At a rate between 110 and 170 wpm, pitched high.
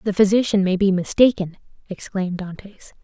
Yes: average, 140 wpm; high, 195 Hz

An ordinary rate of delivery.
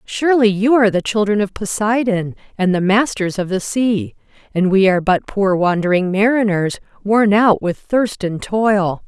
Yes: average, 170 wpm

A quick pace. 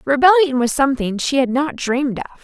No: average, 195 wpm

